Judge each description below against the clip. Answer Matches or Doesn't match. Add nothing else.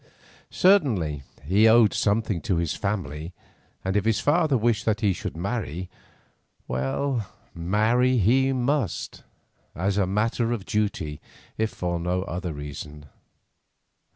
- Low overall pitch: Matches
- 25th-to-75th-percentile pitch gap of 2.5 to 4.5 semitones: Doesn't match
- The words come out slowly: Matches